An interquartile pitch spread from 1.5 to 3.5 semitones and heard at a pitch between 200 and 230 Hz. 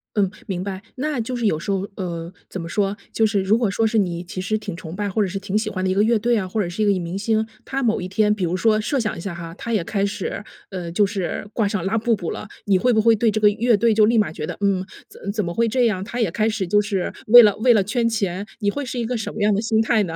Yes: average, 2.9 semitones; high, 205 Hz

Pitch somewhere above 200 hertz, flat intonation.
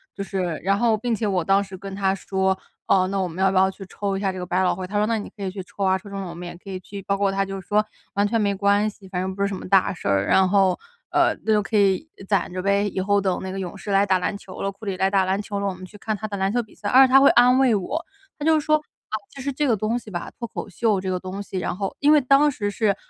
No: high, 195 Hz; narrow, 2.1 semitones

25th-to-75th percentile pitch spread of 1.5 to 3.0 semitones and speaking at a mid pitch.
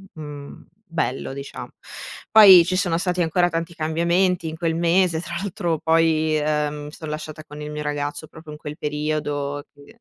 Yes: narrow, 2.4 semitones; medium, 155 Hz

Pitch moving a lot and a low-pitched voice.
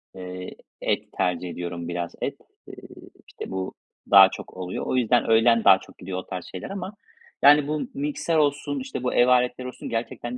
Yes: wide, 7.8 semitones; low, 120 Hz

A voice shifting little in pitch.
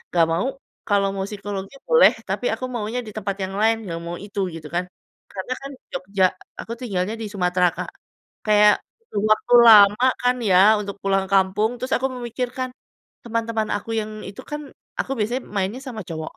No: average, 3.7 semitones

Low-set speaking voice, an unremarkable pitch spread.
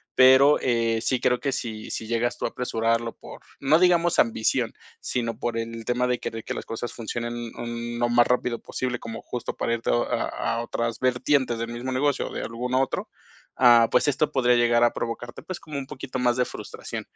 No: low, 120 Hz; narrow, 1.7 semitones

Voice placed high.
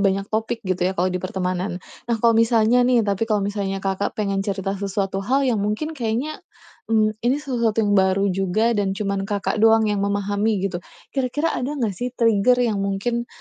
Yes: high, 210 Hz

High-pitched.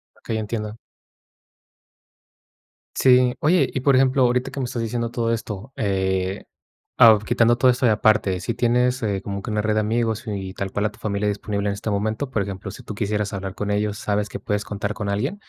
No: low, 105 Hz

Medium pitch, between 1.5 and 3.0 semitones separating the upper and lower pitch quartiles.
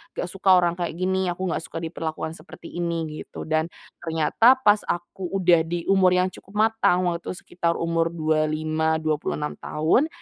Yes: medium, 170 Hz; narrow, 2.5 semitones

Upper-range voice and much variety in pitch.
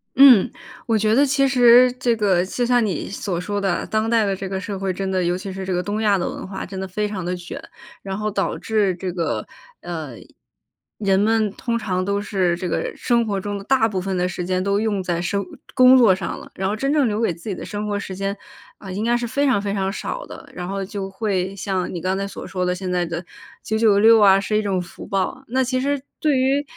No: high, 200 Hz; average, 3.2 semitones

